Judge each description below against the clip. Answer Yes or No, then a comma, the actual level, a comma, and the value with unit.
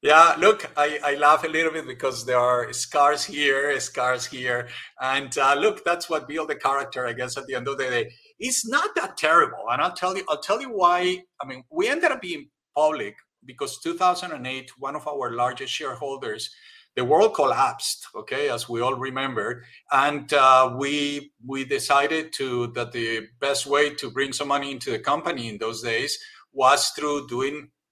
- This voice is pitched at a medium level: Yes, medium, 145 Hz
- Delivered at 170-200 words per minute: Yes, average, 190 wpm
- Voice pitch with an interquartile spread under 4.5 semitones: Yes, average, 3.4 semitones